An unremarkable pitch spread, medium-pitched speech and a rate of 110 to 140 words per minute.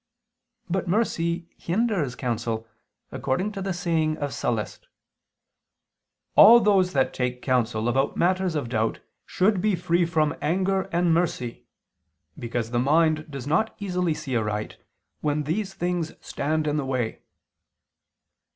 No: wide, 6.2 semitones; medium, 160 Hz; slow, 135 wpm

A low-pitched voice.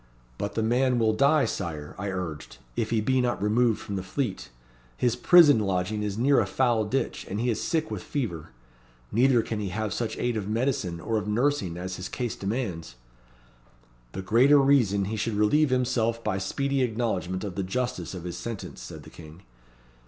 Yes: low, 110 Hz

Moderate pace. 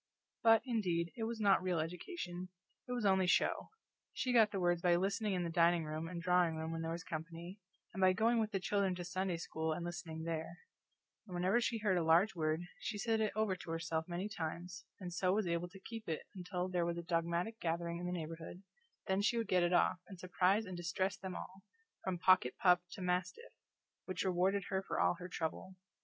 No: fast, 220 wpm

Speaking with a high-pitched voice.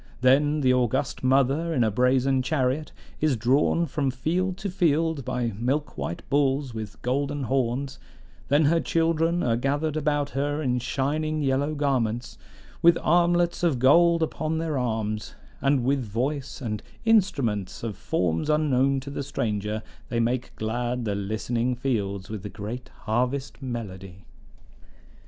No: low, 135 Hz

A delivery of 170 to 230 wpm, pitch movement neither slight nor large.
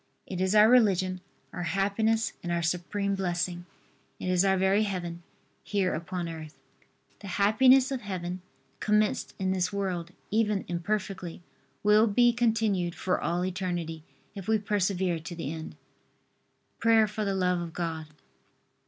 No: average, 145 wpm; average, 3.2 semitones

